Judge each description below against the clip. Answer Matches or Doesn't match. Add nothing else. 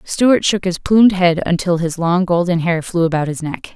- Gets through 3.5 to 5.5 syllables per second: Matches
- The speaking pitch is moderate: Matches